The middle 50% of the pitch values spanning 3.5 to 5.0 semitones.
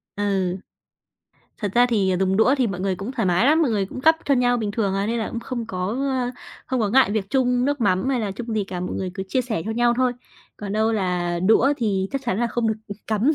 Yes: average, 4.1 semitones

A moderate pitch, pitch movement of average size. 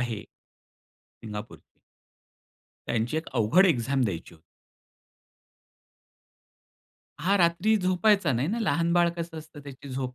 No: medium, 155 Hz; wide, 6.4 semitones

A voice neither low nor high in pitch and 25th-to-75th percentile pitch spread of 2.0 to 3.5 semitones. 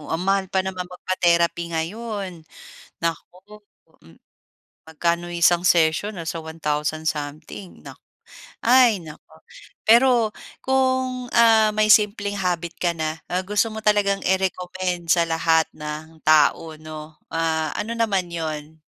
No: medium, 175 Hz; average, 4.5 semitones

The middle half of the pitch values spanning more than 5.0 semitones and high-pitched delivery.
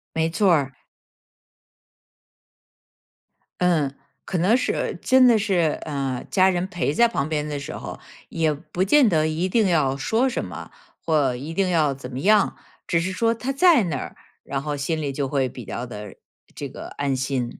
No: wide, 5.5 semitones; medium, 160 Hz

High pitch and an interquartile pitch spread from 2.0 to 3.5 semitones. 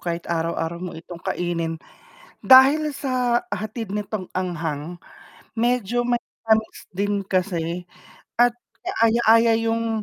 No: high, 205 Hz; wide, 5.6 semitones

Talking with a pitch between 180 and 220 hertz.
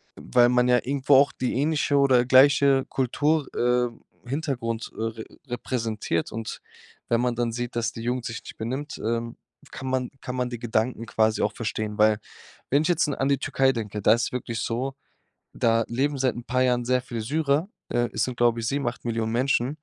No: low, 125 Hz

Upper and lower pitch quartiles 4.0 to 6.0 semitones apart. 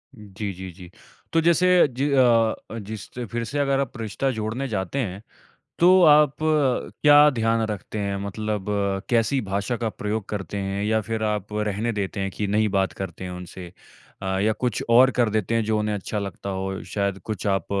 No: average, 3.5 semitones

